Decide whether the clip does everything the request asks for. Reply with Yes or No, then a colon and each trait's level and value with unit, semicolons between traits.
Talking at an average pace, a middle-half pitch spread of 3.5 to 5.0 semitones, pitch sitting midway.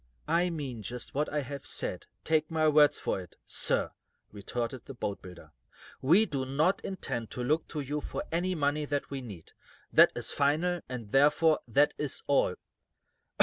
Yes: average, 170 wpm; average, 3.9 semitones; medium, 145 Hz